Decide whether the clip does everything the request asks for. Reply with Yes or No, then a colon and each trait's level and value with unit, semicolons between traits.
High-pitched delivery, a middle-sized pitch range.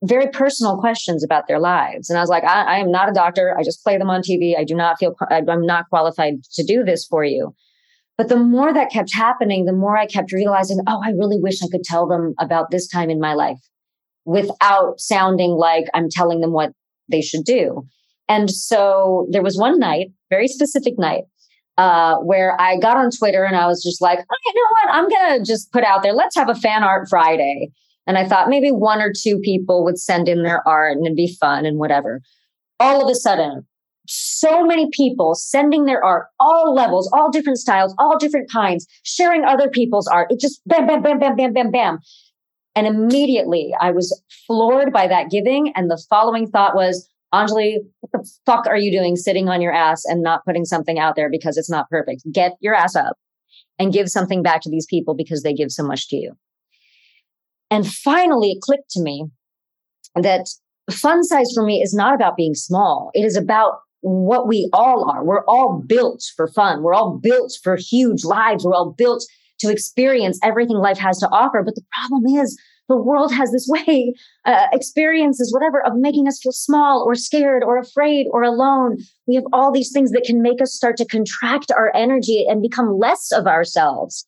No: high, 205 Hz; wide, 6.3 semitones